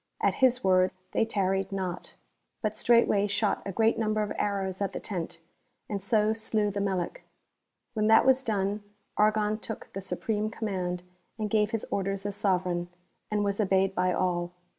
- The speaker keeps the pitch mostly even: Yes, narrow, 2.2 semitones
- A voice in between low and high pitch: No, high, 205 Hz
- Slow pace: No, average, 170 wpm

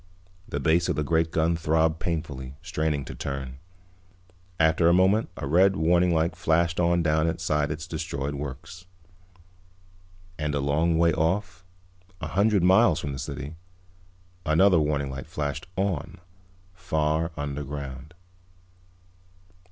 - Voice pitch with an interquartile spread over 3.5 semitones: No, average, 2.9 semitones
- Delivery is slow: Yes, slow, 130 wpm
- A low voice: Yes, very low, 80 Hz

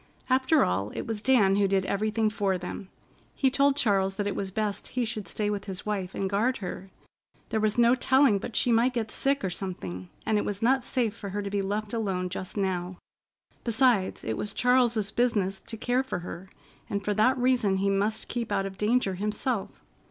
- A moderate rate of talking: No, fast, 210 wpm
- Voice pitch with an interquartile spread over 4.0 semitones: No, average, 3.7 semitones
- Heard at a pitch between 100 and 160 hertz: No, high, 210 Hz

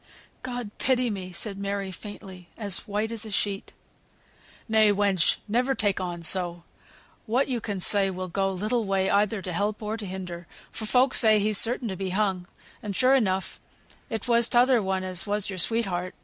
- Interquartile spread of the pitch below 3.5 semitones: Yes, average, 2.9 semitones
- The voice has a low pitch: No, high, 205 Hz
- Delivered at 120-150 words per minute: No, average, 185 wpm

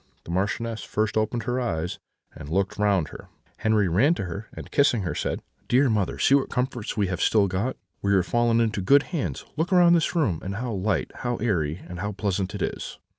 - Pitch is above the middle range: No, low, 105 Hz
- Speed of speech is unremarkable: No, fast, 215 wpm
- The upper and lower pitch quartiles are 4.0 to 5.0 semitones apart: Yes, average, 4.4 semitones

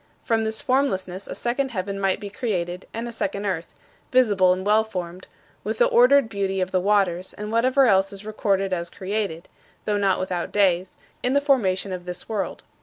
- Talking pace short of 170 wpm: No, average, 190 wpm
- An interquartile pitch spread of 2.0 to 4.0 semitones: Yes, average, 3.2 semitones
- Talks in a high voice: Yes, high, 200 Hz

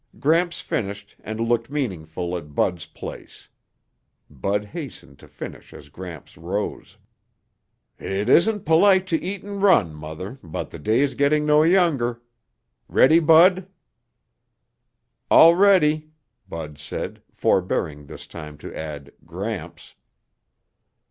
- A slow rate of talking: Yes, slow, 115 wpm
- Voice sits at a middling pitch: No, low, 115 Hz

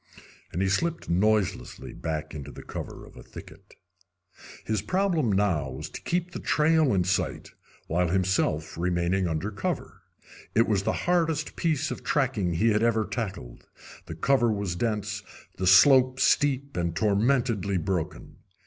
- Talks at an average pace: Yes, average, 150 wpm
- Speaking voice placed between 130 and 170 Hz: No, low, 105 Hz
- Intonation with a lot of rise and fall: Yes, wide, 6.6 semitones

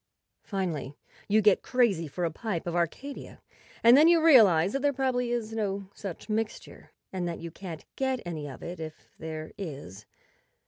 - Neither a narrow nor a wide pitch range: No, wide, 6.5 semitones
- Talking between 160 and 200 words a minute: Yes, average, 175 wpm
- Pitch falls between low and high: No, high, 195 Hz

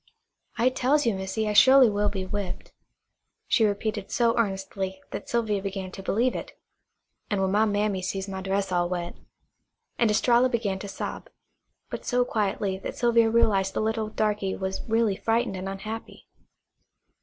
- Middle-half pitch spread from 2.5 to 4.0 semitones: Yes, average, 2.9 semitones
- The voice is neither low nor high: No, high, 205 Hz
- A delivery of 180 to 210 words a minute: No, average, 165 wpm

